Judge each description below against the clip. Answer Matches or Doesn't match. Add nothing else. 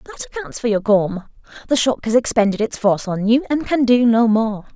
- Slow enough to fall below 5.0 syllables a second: Doesn't match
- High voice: Matches